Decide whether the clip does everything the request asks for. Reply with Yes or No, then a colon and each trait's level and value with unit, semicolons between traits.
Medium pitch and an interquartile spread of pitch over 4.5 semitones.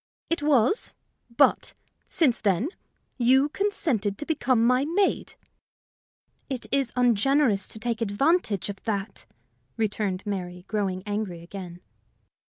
No: high, 225 Hz; wide, 5.5 semitones